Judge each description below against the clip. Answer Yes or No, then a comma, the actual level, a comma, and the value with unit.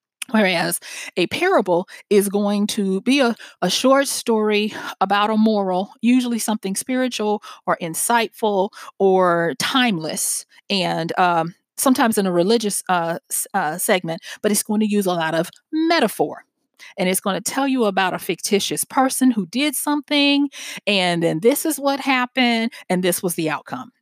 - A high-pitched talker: Yes, high, 205 Hz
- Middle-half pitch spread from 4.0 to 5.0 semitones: No, wide, 5.6 semitones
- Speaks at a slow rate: No, average, 155 wpm